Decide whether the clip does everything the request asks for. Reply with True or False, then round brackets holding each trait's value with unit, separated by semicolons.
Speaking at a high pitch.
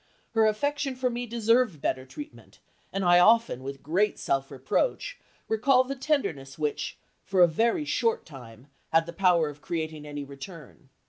False (180 Hz)